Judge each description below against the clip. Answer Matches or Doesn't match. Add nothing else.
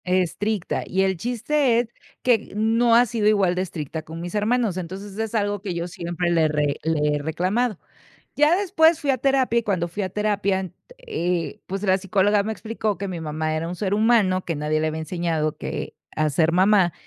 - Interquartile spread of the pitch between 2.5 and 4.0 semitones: Doesn't match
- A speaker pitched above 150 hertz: Matches